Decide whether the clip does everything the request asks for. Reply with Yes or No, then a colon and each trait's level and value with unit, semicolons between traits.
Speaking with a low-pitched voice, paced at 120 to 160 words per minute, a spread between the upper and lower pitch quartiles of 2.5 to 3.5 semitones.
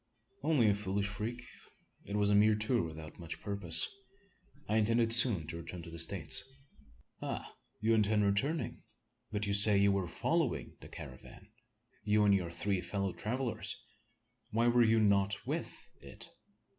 Yes: low, 105 Hz; average, 155 wpm; average, 2.8 semitones